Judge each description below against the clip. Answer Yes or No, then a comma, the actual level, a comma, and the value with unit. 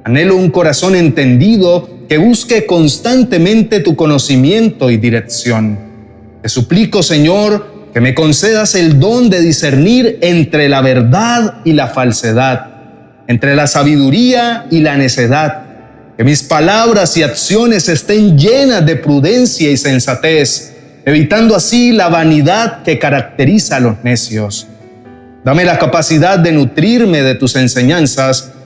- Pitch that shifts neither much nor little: No, wide, 6.3 semitones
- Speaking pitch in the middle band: Yes, medium, 150 Hz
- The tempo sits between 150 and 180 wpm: No, average, 130 wpm